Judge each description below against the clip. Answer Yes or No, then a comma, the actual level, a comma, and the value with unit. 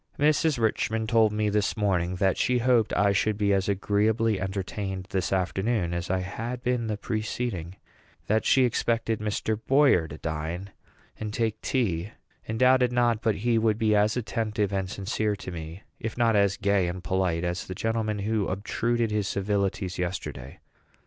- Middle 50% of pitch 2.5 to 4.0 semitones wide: Yes, average, 3.1 semitones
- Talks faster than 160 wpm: Yes, average, 170 wpm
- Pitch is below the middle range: Yes, low, 105 Hz